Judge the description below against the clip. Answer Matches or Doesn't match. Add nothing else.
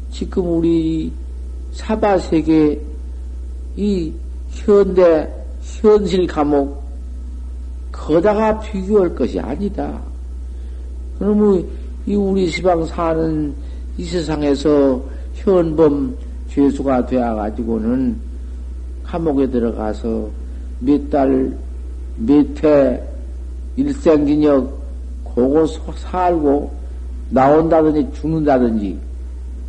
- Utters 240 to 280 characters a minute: Doesn't match